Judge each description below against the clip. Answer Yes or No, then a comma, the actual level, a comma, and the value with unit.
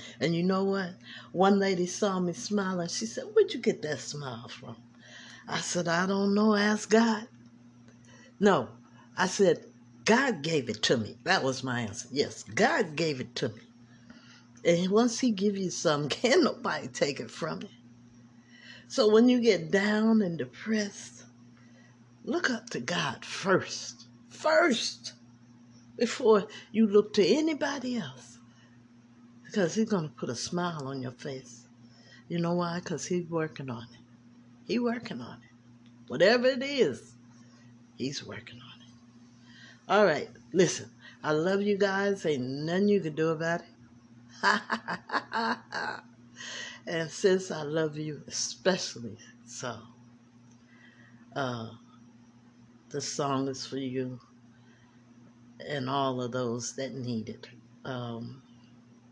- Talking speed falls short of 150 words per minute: Yes, slow, 135 wpm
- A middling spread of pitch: No, wide, 7.4 semitones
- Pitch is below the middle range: Yes, low, 125 Hz